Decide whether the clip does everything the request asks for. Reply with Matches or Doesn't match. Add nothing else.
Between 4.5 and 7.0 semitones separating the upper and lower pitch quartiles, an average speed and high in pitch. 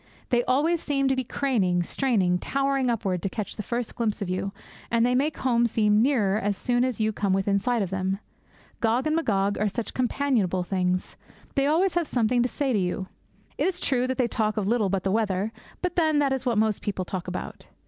Doesn't match